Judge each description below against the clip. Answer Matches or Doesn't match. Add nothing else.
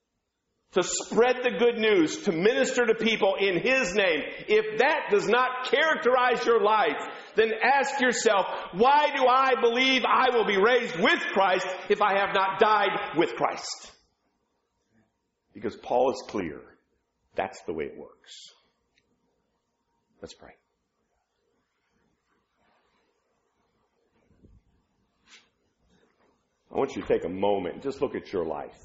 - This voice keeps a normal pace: Doesn't match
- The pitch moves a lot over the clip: Matches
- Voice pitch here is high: Matches